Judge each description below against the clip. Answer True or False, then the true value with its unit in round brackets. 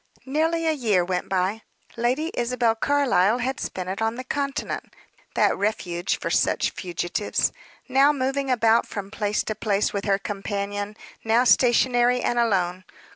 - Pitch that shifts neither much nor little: True (4.4 semitones)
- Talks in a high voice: True (225 Hz)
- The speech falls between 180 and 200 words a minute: False (150 wpm)